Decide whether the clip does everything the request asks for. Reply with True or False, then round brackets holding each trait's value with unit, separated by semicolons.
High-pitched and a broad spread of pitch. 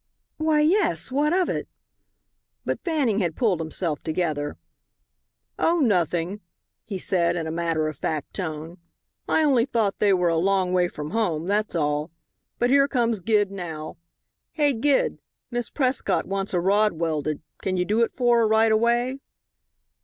True (195 Hz; 6.3 semitones)